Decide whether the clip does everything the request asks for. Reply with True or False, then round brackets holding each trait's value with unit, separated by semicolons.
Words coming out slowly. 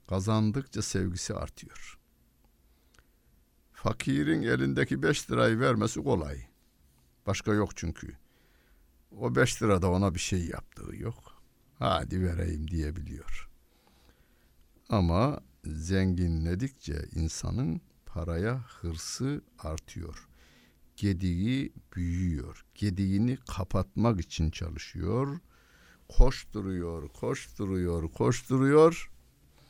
True (75 wpm)